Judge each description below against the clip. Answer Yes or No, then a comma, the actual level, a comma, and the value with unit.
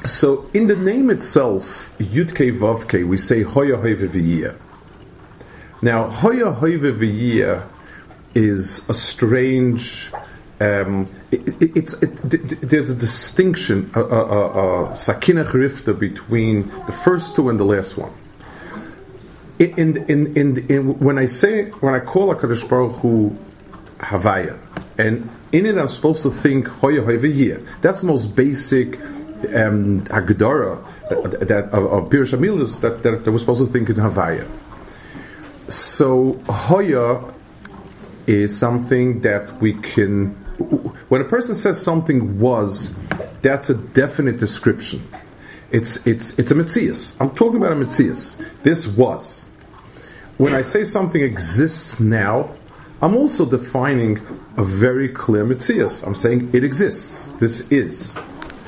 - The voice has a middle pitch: No, low, 125 Hz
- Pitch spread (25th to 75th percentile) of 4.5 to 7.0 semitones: Yes, average, 5.1 semitones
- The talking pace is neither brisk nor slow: No, slow, 125 wpm